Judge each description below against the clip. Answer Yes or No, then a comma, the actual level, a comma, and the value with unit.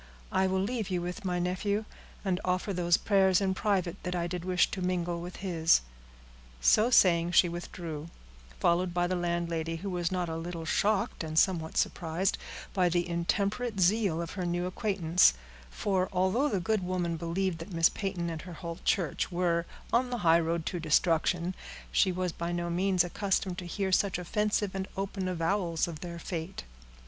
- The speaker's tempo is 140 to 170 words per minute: No, average, 180 wpm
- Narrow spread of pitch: Yes, narrow, 2.1 semitones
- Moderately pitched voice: Yes, medium, 180 Hz